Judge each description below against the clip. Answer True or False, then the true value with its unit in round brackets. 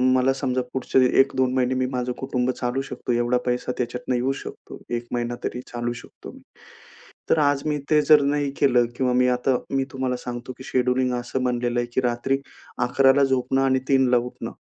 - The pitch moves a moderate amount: False (1.4 semitones)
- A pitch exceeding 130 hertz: False (125 Hz)